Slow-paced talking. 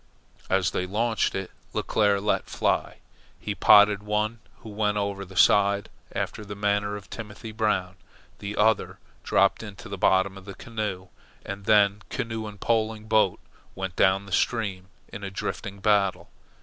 No: average, 160 wpm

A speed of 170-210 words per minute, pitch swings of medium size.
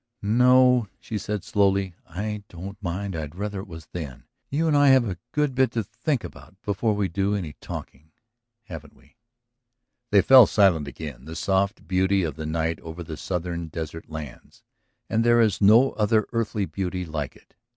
Yes: average, 180 wpm; average, 4.9 semitones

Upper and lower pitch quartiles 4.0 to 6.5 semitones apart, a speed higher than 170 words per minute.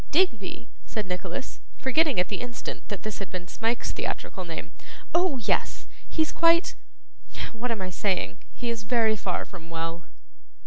No: wide, 5.4 semitones; average, 160 wpm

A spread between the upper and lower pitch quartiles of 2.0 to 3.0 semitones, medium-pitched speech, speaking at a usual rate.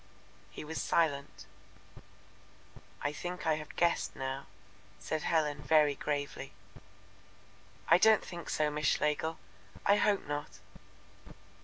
No: narrow, 2.5 semitones; medium, 150 Hz; slow, 115 wpm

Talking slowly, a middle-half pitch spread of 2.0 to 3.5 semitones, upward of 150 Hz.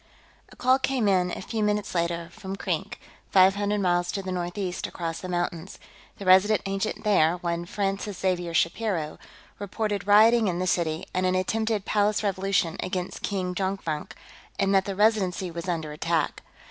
No: average, 170 wpm; average, 2.7 semitones; high, 190 Hz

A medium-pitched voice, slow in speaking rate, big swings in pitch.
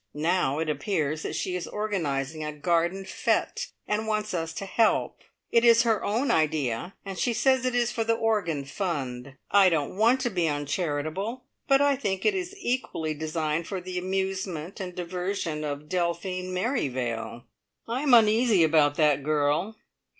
No: medium, 180 Hz; average, 165 wpm; wide, 6.0 semitones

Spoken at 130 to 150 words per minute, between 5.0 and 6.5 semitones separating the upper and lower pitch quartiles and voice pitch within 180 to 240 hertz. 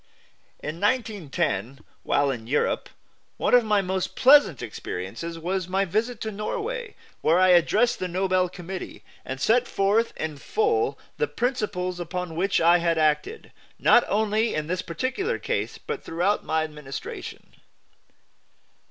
Yes: average, 140 wpm; wide, 5.6 semitones; medium, 185 Hz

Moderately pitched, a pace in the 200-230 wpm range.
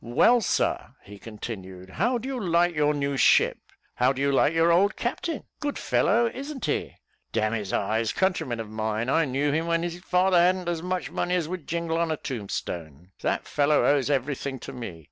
Yes: medium, 150 Hz; fast, 205 wpm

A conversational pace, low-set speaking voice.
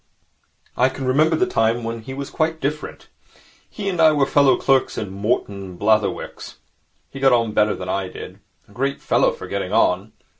Yes: average, 190 wpm; low, 130 Hz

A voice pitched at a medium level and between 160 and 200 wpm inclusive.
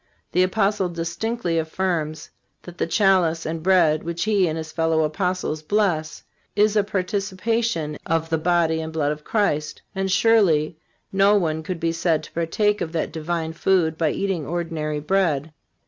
Yes: medium, 170 Hz; average, 165 wpm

